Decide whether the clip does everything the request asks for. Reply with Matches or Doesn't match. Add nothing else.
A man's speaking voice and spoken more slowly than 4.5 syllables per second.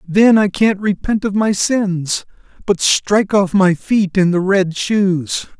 Matches